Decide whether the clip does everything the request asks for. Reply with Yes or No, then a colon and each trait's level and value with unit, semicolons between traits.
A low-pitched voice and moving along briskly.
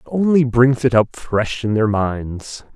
No: low, 120 Hz; average, 195 wpm